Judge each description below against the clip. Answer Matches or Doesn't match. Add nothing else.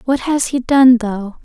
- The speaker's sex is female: Matches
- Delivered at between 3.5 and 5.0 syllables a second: Matches